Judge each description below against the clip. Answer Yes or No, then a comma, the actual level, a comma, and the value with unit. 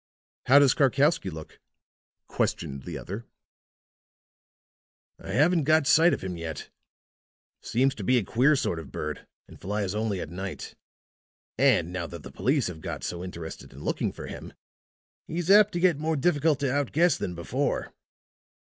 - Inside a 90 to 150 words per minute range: No, average, 165 wpm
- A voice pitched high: No, low, 125 Hz